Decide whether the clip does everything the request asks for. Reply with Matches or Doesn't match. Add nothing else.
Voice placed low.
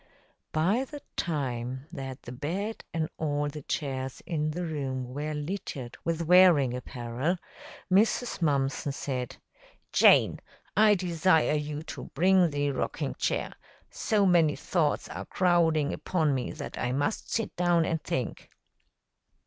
Doesn't match